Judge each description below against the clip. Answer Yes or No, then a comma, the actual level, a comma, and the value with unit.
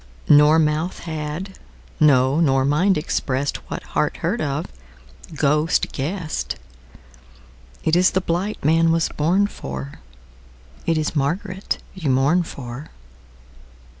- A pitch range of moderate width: No, wide, 7.5 semitones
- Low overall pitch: No, medium, 150 Hz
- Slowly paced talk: Yes, slow, 105 wpm